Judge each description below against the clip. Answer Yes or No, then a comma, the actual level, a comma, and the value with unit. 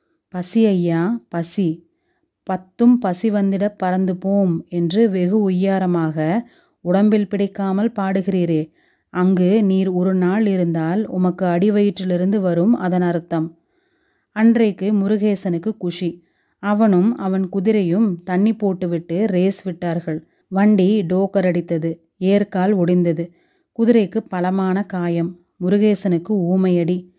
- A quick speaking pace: No, average, 100 wpm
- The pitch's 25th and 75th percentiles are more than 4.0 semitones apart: No, average, 2.8 semitones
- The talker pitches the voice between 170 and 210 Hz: Yes, high, 190 Hz